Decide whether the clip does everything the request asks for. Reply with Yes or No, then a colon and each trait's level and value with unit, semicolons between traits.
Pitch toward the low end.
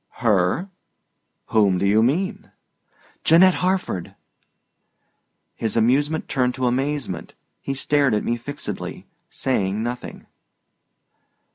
Yes: low, 125 Hz